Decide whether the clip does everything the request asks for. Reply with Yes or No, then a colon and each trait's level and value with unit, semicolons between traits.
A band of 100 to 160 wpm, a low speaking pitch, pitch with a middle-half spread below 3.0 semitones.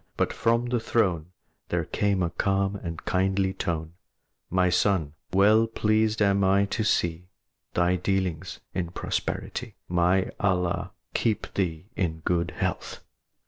Yes: slow, 135 wpm; very low, 95 Hz; narrow, 2.6 semitones